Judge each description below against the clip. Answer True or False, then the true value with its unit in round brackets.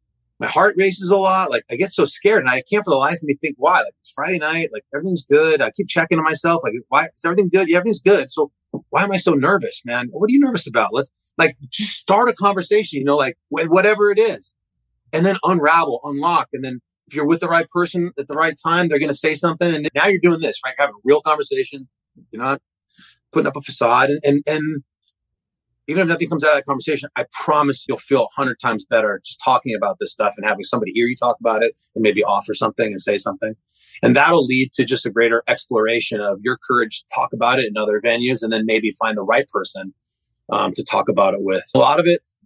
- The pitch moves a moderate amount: False (5.9 semitones)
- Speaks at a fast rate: True (250 wpm)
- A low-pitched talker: False (155 Hz)